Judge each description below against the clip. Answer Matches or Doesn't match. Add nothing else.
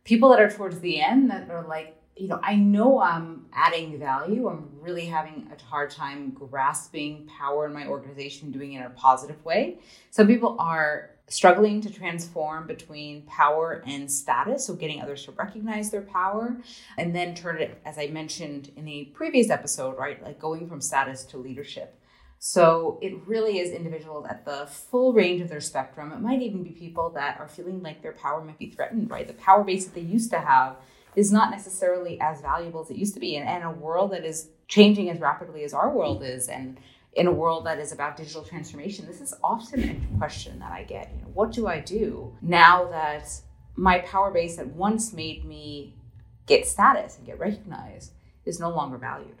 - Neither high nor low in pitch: Matches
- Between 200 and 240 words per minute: Matches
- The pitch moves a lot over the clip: Doesn't match